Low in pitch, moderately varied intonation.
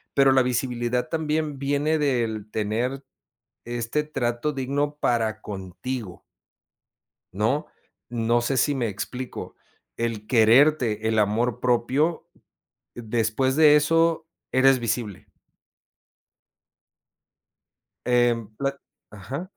Yes: low, 125 Hz; average, 3.8 semitones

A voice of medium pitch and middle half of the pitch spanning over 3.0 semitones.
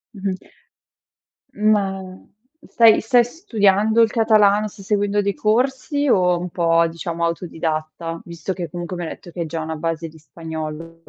Yes: medium, 180 Hz; average, 4.2 semitones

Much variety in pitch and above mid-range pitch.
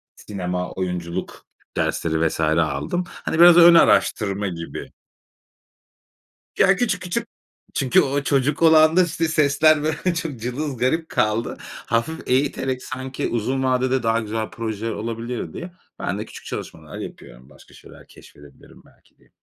No: wide, 7.0 semitones; low, 130 Hz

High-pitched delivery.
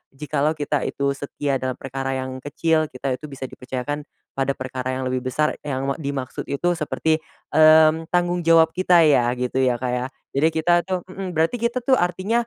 No: medium, 145 Hz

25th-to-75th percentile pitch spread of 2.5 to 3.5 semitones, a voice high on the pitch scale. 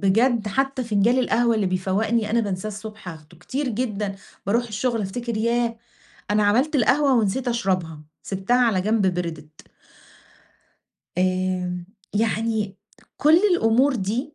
No: average, 4.1 semitones; high, 215 Hz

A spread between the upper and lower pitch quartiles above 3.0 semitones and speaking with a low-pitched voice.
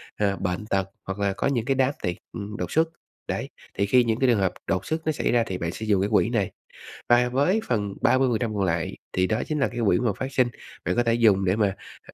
Yes: average, 4.4 semitones; low, 110 Hz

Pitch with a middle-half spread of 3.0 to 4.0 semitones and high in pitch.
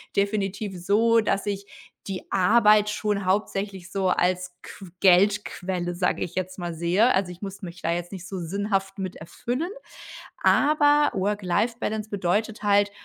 No: narrow, 2.5 semitones; high, 195 Hz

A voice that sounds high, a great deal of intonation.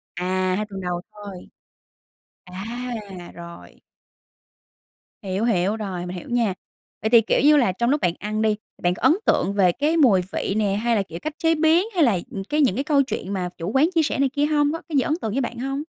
Yes: high, 220 Hz; wide, 6.9 semitones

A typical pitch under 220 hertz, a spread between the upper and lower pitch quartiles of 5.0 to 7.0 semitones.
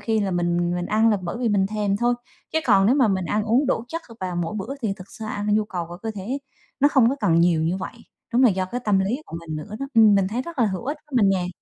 No: high, 205 Hz; average, 4.5 semitones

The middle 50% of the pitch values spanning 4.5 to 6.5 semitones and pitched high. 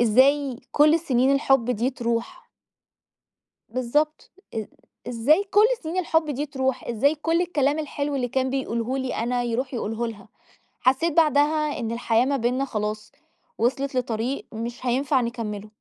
No: average, 3.6 semitones; very high, 260 Hz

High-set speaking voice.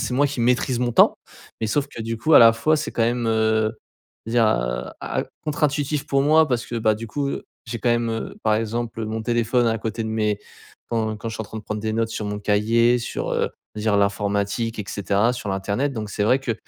No: low, 115 Hz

